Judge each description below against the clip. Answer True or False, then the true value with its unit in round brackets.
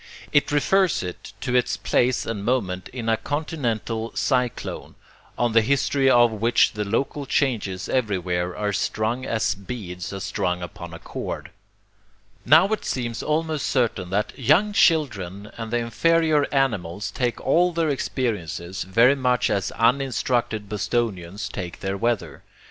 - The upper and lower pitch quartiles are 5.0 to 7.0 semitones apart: True (5.3 semitones)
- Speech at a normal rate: True (145 wpm)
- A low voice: True (115 Hz)